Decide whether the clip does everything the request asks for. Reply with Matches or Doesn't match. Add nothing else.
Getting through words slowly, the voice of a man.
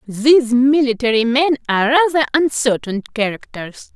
Doesn't match